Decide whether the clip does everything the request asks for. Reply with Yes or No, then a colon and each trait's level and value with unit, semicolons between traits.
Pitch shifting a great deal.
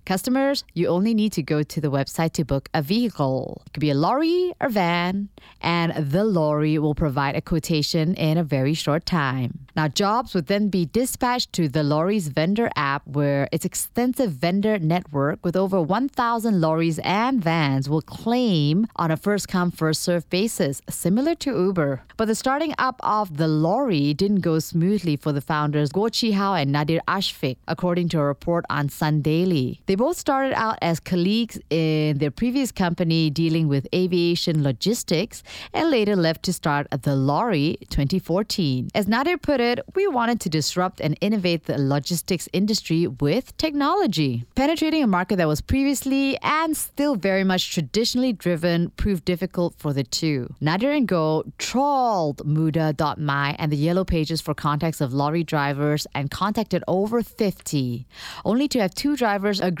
Yes: wide, 5.8 semitones